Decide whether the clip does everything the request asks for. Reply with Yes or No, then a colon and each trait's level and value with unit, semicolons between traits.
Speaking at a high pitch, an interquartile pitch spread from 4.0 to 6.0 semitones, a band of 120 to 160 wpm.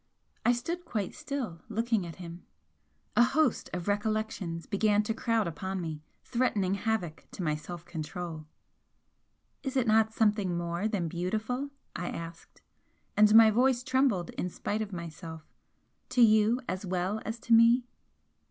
Yes: high, 210 Hz; average, 4.7 semitones; average, 150 wpm